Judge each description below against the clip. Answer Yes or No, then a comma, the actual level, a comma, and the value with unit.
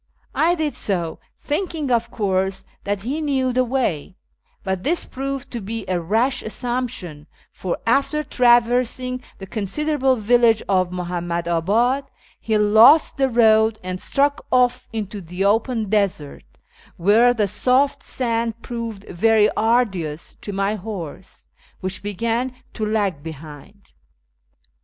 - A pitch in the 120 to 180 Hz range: No, high, 220 Hz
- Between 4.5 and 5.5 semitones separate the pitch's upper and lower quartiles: Yes, average, 4.8 semitones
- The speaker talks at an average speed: No, slow, 130 wpm